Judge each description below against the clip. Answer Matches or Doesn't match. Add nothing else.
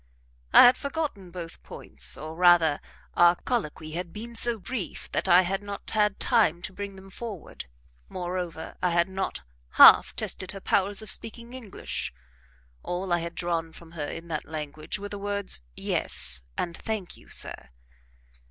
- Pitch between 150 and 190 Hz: Matches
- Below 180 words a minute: Matches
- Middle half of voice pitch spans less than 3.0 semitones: Doesn't match